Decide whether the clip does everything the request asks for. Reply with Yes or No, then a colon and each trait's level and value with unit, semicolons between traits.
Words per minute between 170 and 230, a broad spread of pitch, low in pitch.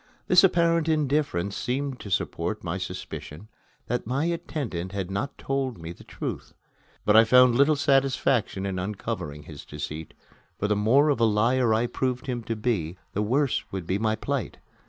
Yes: average, 175 wpm; wide, 5.8 semitones; low, 115 Hz